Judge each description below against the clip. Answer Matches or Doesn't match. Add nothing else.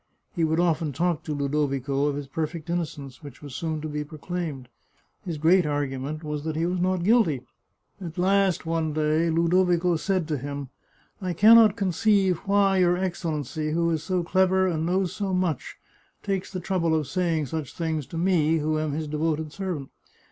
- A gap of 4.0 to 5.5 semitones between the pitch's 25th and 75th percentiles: Doesn't match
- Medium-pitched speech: Matches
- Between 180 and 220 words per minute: Matches